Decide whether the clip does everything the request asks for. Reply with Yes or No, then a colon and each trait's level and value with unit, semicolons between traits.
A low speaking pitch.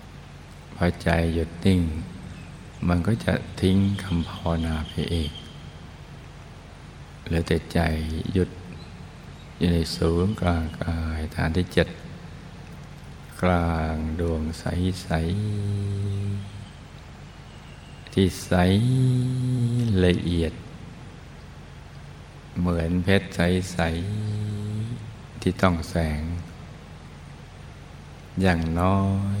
Yes: very low, 85 Hz